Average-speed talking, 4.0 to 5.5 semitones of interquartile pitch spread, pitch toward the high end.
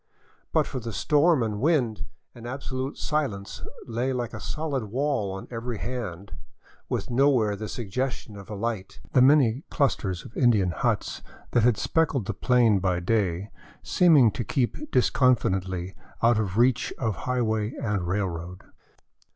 No: average, 150 wpm; average, 4.5 semitones; low, 115 Hz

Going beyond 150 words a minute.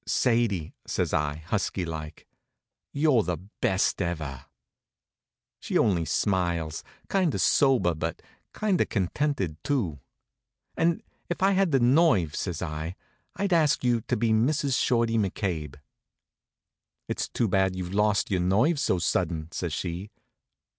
No: slow, 135 wpm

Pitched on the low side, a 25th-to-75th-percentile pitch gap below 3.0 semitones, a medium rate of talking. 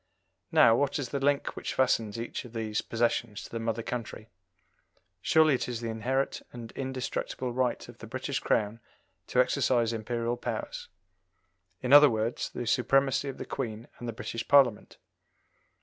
Yes: low, 120 Hz; narrow, 2.6 semitones; average, 165 wpm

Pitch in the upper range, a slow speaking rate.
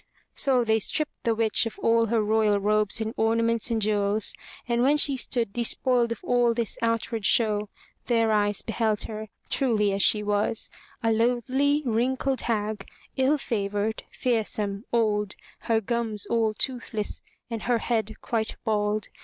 No: high, 225 Hz; average, 155 wpm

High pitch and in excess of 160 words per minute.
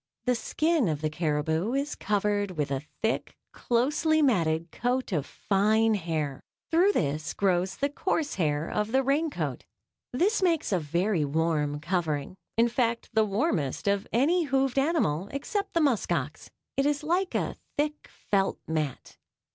No: high, 210 Hz; average, 155 wpm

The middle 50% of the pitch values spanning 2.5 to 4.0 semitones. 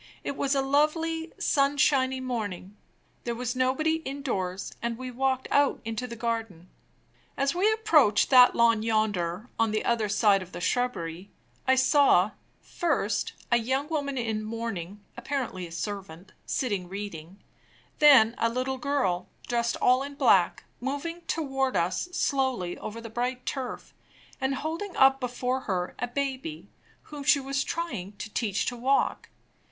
No: average, 4.7 semitones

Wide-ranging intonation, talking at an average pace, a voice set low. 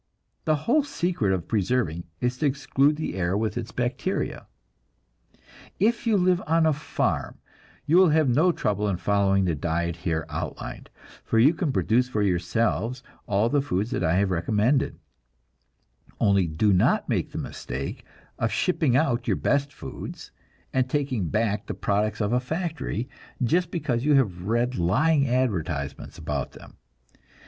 Yes: wide, 7.5 semitones; average, 155 wpm; low, 120 Hz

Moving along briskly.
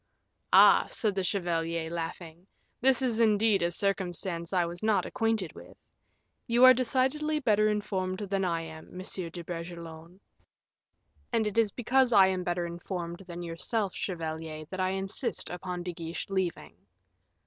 No: average, 150 wpm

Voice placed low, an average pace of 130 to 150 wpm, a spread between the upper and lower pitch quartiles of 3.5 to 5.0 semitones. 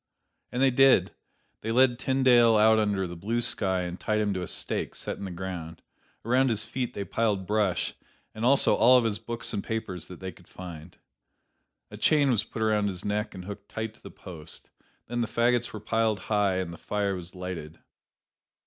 No: low, 105 Hz; fast, 205 wpm; average, 3.9 semitones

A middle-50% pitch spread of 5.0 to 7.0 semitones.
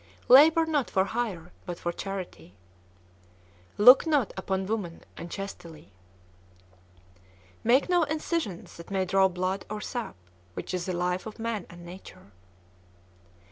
Yes: average, 5.3 semitones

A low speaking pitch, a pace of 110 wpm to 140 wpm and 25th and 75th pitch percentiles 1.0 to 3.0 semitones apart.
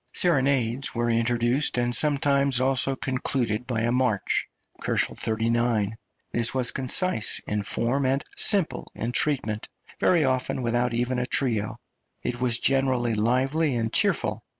Yes: low, 125 Hz; slow, 135 wpm; narrow, 2.5 semitones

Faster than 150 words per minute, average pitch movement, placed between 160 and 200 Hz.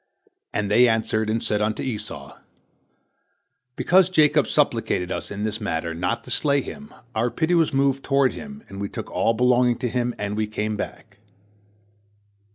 No: average, 165 wpm; average, 4.7 semitones; low, 115 Hz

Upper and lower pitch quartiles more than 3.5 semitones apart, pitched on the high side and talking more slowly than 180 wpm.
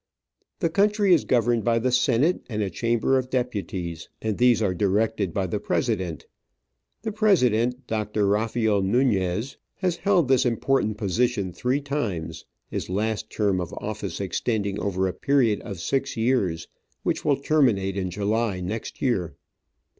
No: average, 4.6 semitones; low, 110 Hz; average, 150 wpm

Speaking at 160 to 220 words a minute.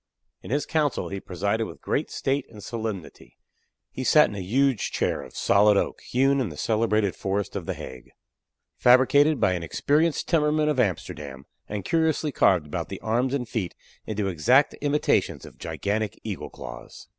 Yes: average, 170 wpm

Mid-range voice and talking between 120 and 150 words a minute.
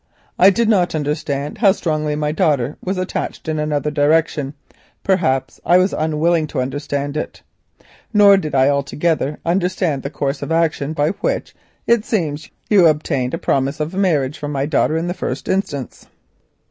No: medium, 155 Hz; average, 165 wpm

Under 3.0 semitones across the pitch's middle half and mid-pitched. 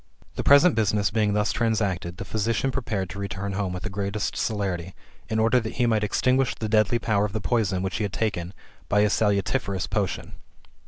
No: narrow, 2.4 semitones; low, 105 Hz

